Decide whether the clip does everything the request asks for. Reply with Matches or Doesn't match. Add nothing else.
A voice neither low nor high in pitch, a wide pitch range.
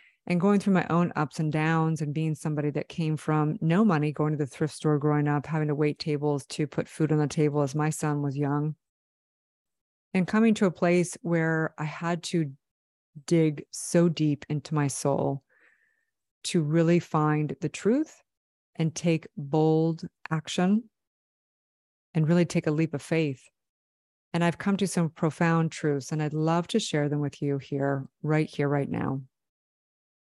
Doesn't match